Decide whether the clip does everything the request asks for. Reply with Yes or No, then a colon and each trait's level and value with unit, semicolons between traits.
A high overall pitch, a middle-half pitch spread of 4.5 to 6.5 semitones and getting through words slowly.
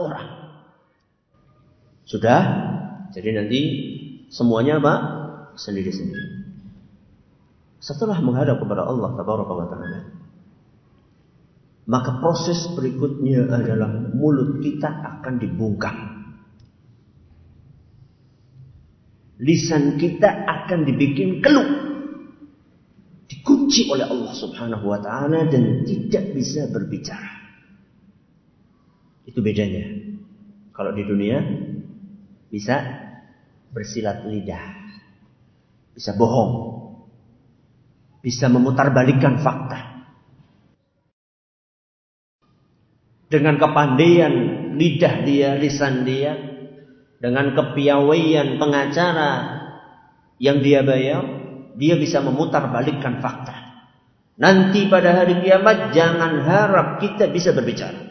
No: medium, 140 Hz; average, 5.1 semitones; slow, 75 wpm